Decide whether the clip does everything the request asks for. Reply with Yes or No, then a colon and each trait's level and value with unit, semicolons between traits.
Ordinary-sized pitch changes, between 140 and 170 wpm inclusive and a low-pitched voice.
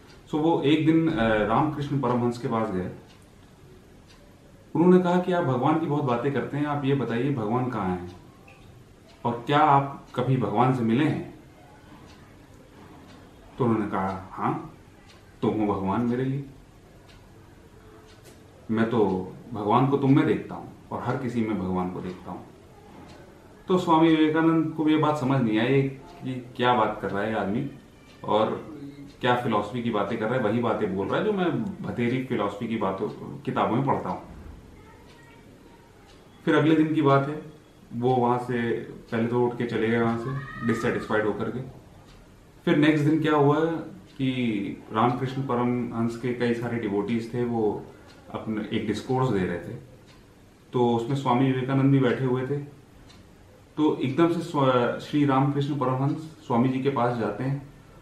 Yes: average, 4.6 semitones; average, 165 wpm; low, 120 Hz